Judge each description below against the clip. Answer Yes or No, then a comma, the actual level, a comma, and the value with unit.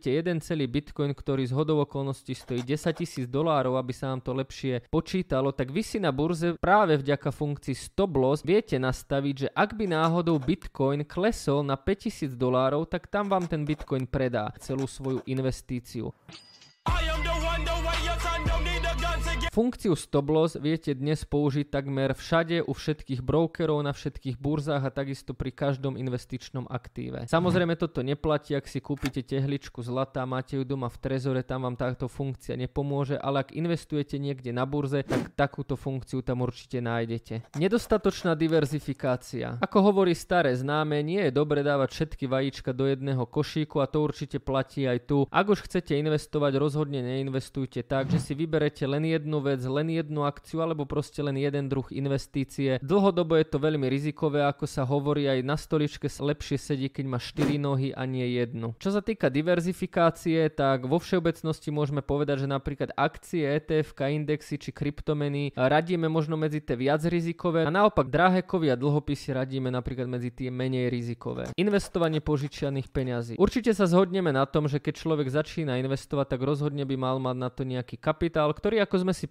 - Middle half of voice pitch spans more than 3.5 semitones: No, average, 3.1 semitones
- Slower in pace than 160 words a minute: No, fast, 165 wpm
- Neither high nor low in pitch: Yes, medium, 145 Hz